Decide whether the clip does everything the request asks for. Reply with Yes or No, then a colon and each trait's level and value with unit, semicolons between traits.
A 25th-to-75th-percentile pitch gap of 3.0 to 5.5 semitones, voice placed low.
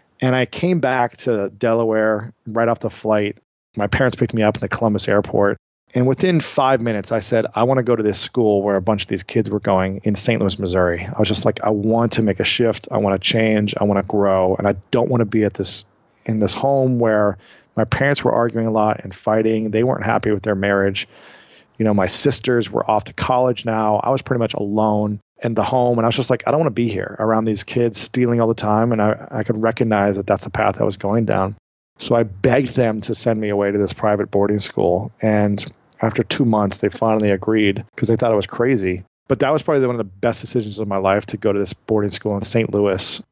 No: narrow, 2.6 semitones; low, 110 Hz